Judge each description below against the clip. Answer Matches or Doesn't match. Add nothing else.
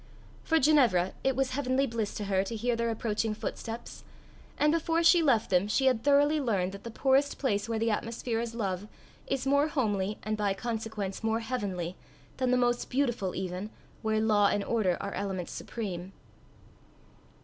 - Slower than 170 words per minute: Doesn't match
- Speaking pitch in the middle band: Doesn't match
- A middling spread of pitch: Matches